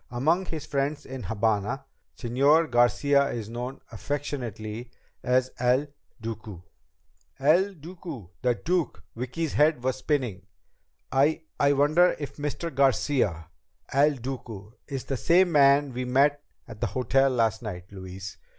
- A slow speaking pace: Yes, slow, 130 wpm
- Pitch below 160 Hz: Yes, low, 135 Hz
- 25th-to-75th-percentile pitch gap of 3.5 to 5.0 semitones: Yes, average, 4.1 semitones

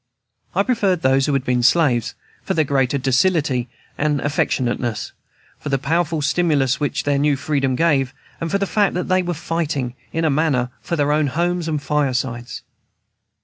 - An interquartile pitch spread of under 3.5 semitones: No, average, 3.9 semitones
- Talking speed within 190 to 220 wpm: No, average, 175 wpm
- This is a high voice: No, medium, 145 Hz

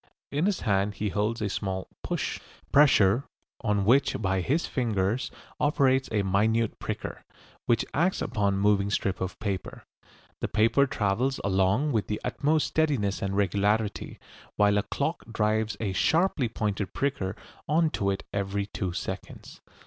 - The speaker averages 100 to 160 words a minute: Yes, average, 150 wpm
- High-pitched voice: No, low, 105 Hz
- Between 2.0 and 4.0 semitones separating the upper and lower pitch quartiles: No, average, 5.0 semitones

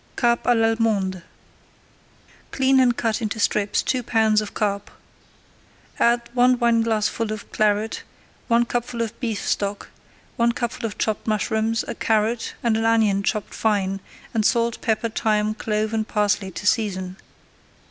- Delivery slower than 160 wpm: Yes, average, 150 wpm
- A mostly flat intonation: Yes, narrow, 1.8 semitones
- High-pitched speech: Yes, high, 220 Hz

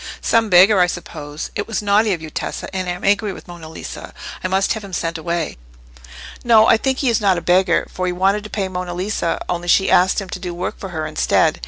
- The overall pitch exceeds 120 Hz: Yes, medium, 185 Hz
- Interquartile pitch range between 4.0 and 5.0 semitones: No, average, 2.7 semitones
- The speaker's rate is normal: No, fast, 245 wpm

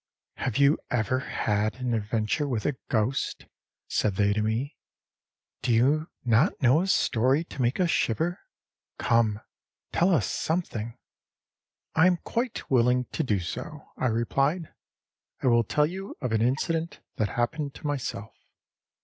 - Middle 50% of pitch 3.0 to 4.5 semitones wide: No, average, 5.3 semitones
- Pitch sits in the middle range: No, low, 125 Hz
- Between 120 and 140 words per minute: No, average, 150 wpm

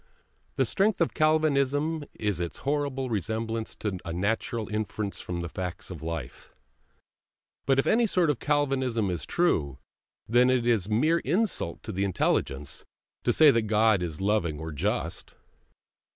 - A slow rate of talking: No, average, 155 wpm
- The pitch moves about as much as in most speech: No, wide, 7.7 semitones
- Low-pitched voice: Yes, low, 110 Hz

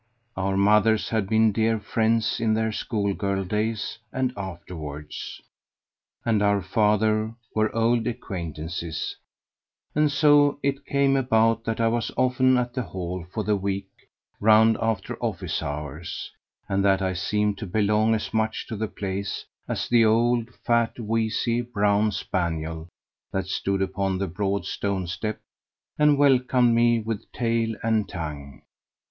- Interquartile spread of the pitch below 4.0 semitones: Yes, average, 2.9 semitones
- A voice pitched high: No, low, 110 Hz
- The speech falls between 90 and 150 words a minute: Yes, average, 145 wpm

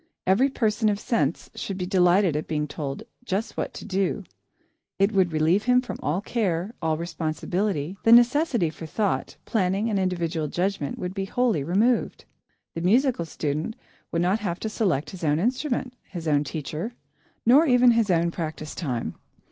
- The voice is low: No, medium, 185 Hz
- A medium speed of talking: Yes, average, 170 wpm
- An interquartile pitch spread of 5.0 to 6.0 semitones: Yes, wide, 5.4 semitones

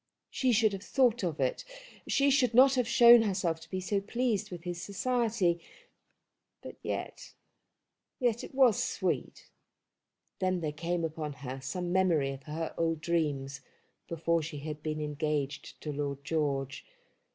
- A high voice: No, medium, 170 Hz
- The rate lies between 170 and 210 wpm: No, average, 150 wpm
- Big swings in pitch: Yes, wide, 6.1 semitones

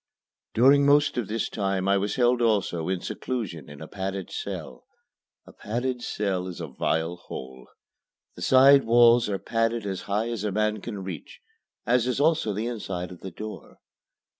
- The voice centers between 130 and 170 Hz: No, low, 105 Hz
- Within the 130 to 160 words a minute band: No, average, 175 wpm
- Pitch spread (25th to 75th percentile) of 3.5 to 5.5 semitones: Yes, average, 4.2 semitones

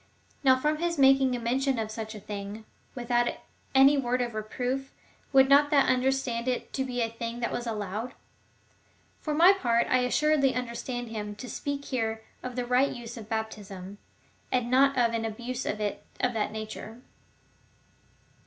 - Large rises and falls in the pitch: No, average, 3.1 semitones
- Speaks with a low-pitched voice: No, high, 245 Hz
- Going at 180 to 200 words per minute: No, average, 170 wpm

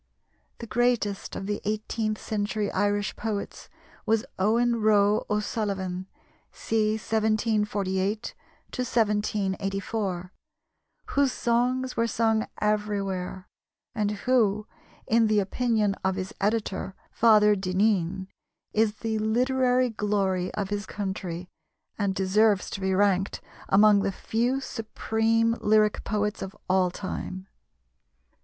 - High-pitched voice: Yes, high, 210 Hz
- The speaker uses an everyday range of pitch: No, narrow, 2.3 semitones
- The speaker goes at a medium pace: No, slow, 110 wpm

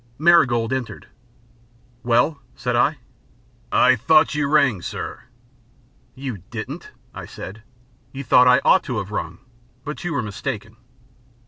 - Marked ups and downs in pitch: No, average, 4.2 semitones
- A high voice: No, low, 125 Hz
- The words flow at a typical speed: No, slow, 130 wpm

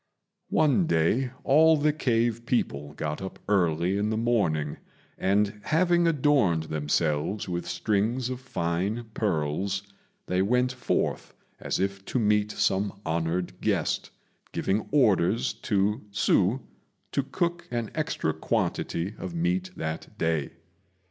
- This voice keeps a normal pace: No, slow, 125 wpm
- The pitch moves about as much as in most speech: No, wide, 6.8 semitones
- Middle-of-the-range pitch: No, low, 105 Hz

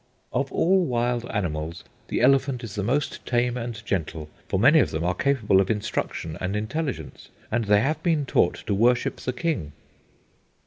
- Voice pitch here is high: No, low, 115 Hz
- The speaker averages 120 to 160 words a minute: No, average, 175 wpm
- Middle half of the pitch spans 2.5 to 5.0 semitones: No, wide, 5.5 semitones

